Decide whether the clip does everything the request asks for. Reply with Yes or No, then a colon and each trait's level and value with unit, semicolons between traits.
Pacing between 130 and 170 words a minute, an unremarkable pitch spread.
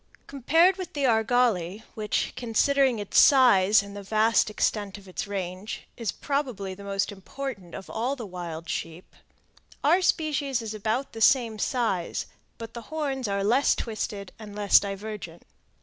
Yes: average, 155 wpm; average, 4.7 semitones